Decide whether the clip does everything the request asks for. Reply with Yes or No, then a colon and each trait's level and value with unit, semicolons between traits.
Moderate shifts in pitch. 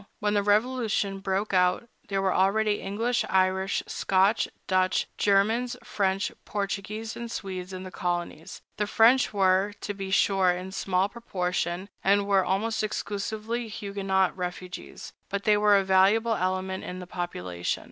No: narrow, 2.0 semitones